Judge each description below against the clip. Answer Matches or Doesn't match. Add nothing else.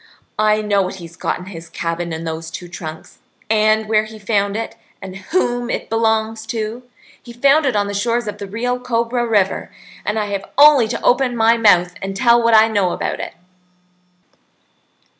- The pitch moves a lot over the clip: Doesn't match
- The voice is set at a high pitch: Matches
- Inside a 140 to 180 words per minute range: Doesn't match